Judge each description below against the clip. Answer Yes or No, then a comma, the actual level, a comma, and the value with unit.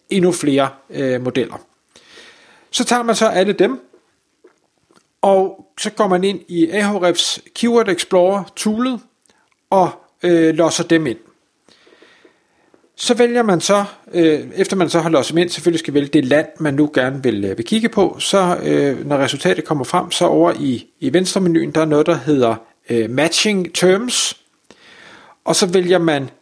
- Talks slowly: No, average, 170 wpm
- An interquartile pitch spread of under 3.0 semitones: No, average, 5.2 semitones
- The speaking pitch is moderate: Yes, medium, 175 Hz